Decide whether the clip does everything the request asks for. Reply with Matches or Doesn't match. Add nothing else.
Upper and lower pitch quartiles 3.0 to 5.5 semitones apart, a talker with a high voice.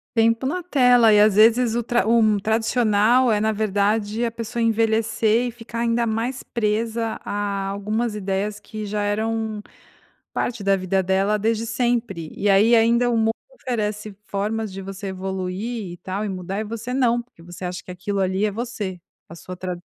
Doesn't match